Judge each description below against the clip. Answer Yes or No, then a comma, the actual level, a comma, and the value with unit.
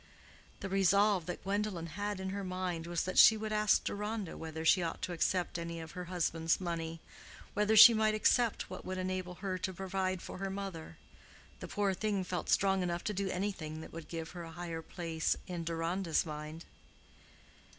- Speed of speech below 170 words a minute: No, average, 185 wpm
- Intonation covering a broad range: No, average, 2.9 semitones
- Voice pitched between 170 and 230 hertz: Yes, medium, 185 Hz